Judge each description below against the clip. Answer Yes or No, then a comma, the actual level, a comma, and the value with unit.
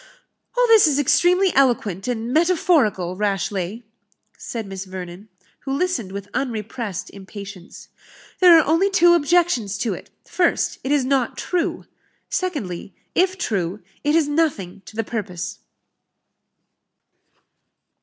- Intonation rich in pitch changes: Yes, wide, 8.8 semitones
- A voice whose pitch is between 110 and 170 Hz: No, high, 240 Hz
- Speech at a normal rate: No, slow, 125 wpm